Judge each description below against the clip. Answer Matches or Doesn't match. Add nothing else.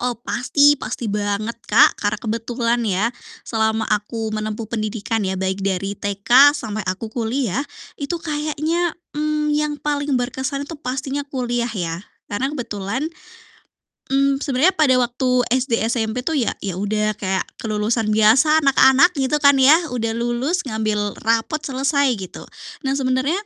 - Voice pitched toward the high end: Matches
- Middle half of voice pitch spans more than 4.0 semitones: Matches